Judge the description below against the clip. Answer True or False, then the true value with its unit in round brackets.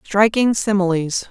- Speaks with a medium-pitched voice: False (200 Hz)